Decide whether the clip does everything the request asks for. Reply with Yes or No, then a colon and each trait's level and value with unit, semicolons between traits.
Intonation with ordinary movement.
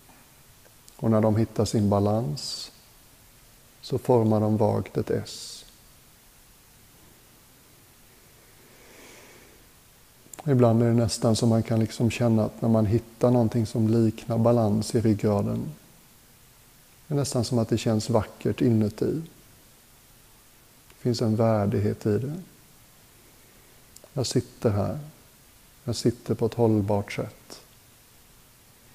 No: narrow, 1.9 semitones